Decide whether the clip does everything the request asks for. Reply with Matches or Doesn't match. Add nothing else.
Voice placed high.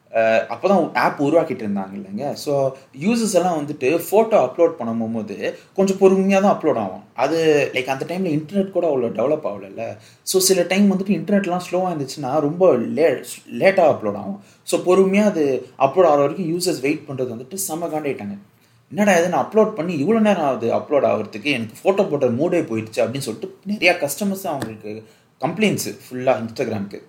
Doesn't match